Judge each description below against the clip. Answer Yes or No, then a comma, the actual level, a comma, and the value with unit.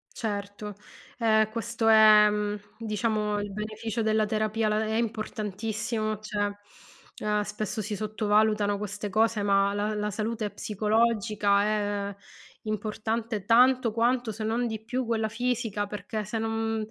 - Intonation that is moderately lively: No, narrow, 1.3 semitones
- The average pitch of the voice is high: Yes, high, 215 Hz